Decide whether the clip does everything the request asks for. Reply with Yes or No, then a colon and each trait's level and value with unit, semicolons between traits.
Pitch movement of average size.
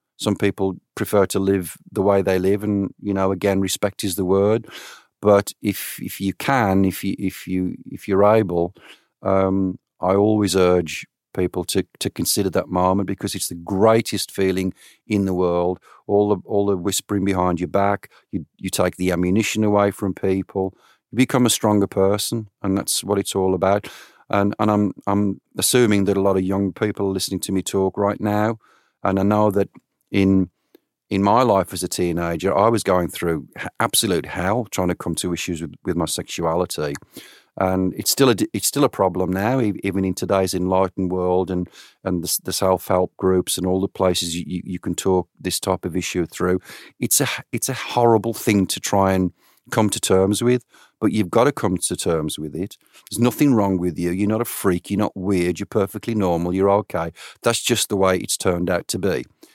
No: narrow, 1.9 semitones